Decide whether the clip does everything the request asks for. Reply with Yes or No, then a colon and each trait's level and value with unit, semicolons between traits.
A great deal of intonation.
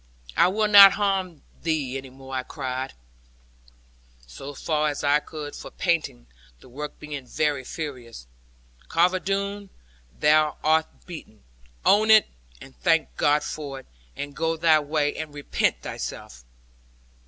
No: average, 3.9 semitones